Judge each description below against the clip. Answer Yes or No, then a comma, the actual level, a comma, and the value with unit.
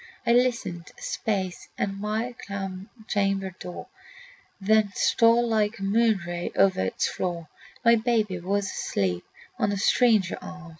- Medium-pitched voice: No, high, 200 Hz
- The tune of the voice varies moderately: Yes, average, 3.4 semitones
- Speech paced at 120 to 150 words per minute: Yes, average, 140 wpm